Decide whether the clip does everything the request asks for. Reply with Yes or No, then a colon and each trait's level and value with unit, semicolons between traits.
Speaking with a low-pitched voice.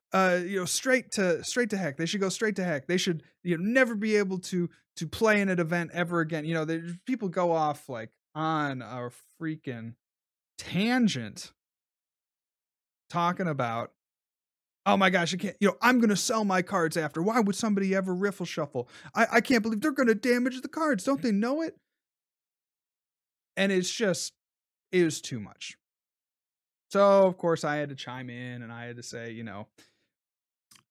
No: medium, 175 Hz